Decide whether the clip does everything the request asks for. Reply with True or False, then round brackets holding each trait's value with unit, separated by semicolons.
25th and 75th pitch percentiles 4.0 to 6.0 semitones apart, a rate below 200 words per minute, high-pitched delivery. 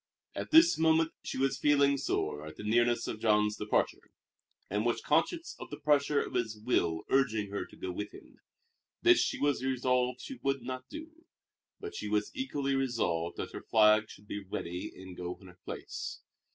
False (5.6 semitones; 190 wpm; 125 Hz)